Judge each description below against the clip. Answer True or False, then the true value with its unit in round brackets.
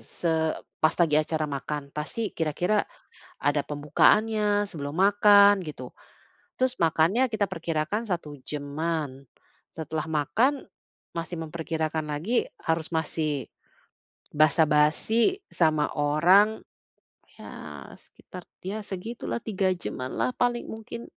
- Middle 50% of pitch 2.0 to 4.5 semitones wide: False (5.3 semitones)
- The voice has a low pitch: False (165 Hz)